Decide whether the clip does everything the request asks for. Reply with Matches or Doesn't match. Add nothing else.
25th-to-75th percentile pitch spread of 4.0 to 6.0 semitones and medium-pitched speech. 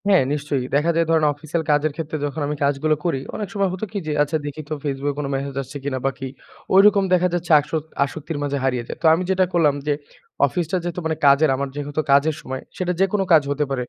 Doesn't match